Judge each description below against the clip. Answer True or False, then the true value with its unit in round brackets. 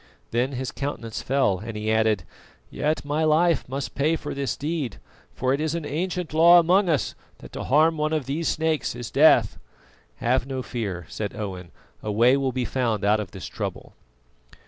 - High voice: False (135 Hz)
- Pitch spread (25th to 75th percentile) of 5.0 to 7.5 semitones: True (5.6 semitones)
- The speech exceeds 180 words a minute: True (190 wpm)